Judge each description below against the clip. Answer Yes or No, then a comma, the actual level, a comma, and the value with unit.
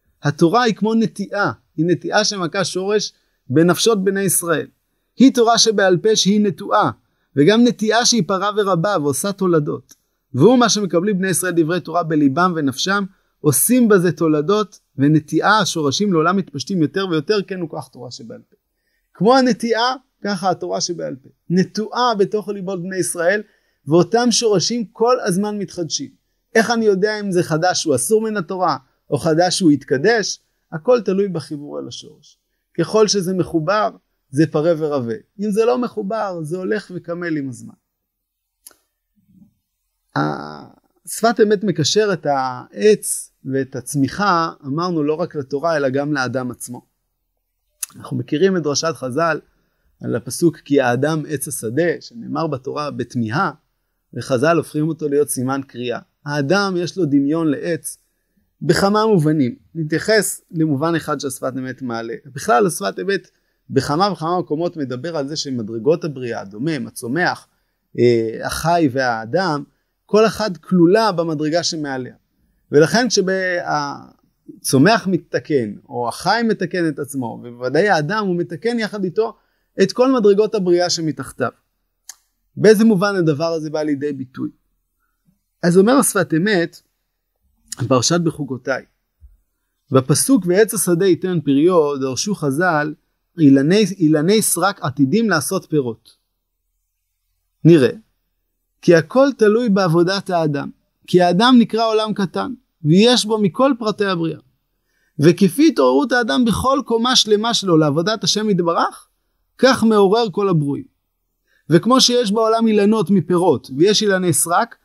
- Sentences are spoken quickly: No, average, 130 wpm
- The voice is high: No, medium, 175 Hz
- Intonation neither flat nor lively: No, wide, 6.0 semitones